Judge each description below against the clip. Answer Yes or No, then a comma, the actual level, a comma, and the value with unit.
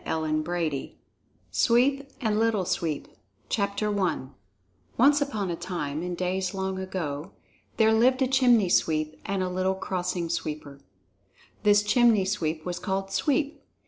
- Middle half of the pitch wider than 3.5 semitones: Yes, average, 4.5 semitones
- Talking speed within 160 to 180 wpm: No, slow, 135 wpm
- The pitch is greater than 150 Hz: Yes, high, 190 Hz